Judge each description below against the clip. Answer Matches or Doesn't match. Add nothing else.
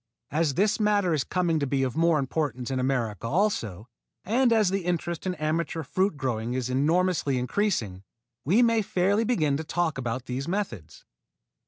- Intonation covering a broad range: Matches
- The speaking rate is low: Doesn't match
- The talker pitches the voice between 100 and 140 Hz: Doesn't match